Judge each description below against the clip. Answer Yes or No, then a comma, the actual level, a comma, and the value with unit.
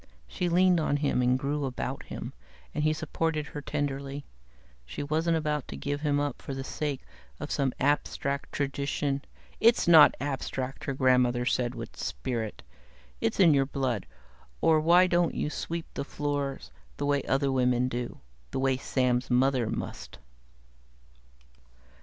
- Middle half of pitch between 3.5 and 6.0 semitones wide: No, narrow, 2.6 semitones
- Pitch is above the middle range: No, medium, 140 Hz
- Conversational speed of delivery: Yes, average, 155 wpm